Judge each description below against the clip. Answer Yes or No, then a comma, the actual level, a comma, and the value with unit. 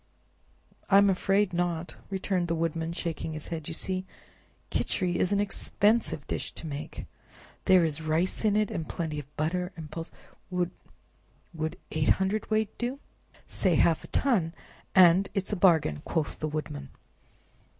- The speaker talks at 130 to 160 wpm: Yes, average, 150 wpm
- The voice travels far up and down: No, average, 3.4 semitones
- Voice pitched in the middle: Yes, medium, 175 Hz